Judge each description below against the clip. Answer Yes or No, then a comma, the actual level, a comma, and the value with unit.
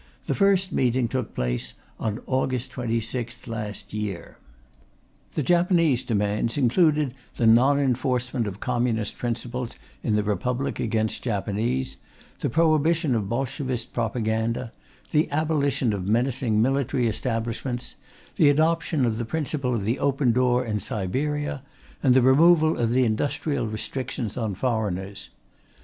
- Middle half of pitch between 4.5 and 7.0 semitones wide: No, average, 3.9 semitones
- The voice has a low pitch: Yes, low, 125 Hz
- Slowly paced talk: Yes, slow, 130 wpm